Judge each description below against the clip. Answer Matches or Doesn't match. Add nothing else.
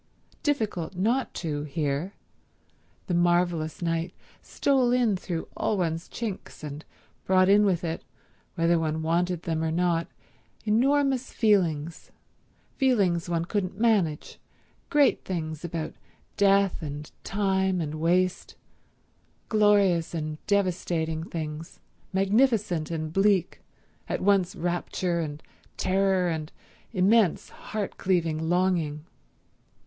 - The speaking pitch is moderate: Matches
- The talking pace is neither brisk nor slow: Doesn't match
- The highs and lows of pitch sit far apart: Doesn't match